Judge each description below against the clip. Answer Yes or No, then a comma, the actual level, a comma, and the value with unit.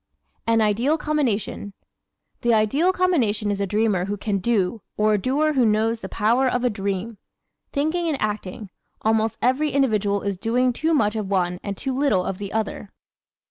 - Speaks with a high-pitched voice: Yes, high, 220 Hz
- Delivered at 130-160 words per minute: No, average, 180 wpm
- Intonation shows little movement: No, average, 4.3 semitones